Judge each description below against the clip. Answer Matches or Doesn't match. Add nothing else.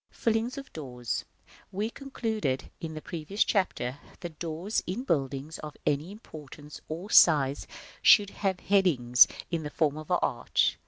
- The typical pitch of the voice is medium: Matches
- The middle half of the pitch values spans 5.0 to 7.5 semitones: Matches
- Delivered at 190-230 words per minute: Doesn't match